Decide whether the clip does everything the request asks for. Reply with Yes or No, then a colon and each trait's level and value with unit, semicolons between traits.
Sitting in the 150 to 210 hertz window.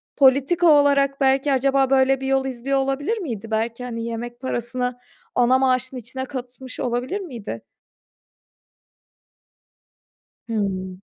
No: very high, 260 Hz